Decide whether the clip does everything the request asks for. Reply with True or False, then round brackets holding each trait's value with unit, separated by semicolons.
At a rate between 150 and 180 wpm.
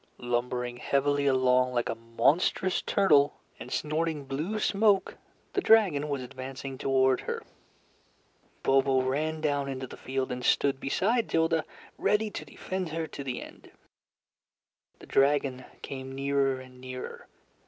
False (135 wpm)